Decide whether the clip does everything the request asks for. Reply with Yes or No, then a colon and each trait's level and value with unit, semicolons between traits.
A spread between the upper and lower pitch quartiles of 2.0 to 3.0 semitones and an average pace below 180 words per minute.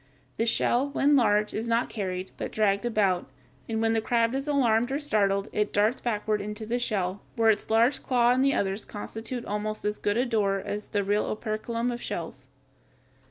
No: average, 2.7 semitones; average, 195 wpm